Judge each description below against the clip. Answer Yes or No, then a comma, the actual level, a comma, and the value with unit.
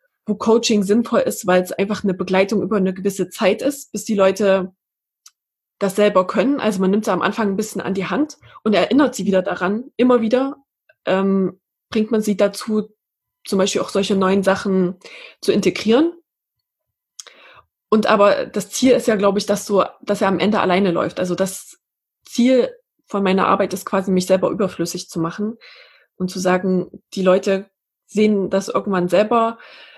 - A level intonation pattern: No, average, 3.0 semitones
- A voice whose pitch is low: No, high, 200 Hz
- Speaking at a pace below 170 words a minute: No, average, 180 wpm